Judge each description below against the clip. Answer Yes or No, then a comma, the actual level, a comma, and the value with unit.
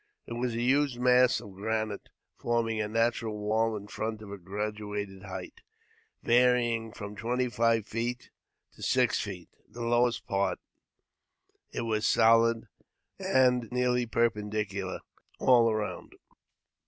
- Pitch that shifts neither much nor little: No, narrow, 2.2 semitones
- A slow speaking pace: Yes, slow, 130 wpm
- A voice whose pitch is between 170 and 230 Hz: No, low, 115 Hz